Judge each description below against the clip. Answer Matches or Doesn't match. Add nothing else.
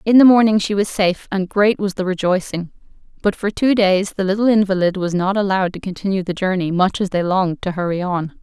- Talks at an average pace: Doesn't match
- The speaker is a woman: Matches